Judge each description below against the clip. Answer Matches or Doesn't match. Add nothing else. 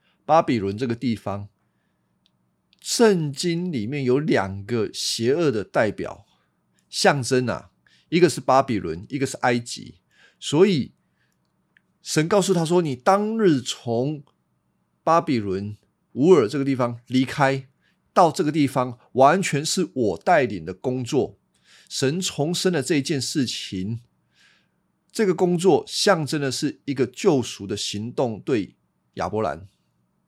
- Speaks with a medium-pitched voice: Doesn't match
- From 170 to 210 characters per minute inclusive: Matches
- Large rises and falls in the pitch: Matches